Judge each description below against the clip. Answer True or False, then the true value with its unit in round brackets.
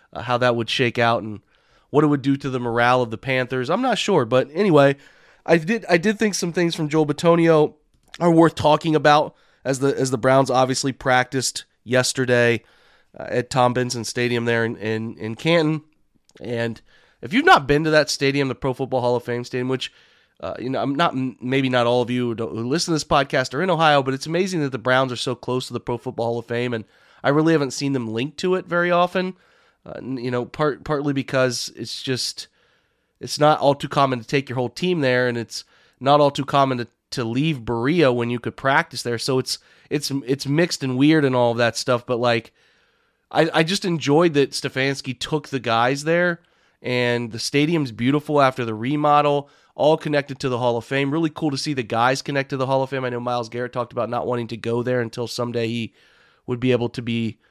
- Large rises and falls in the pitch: False (3.7 semitones)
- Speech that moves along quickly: True (225 wpm)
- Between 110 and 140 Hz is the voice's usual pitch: True (130 Hz)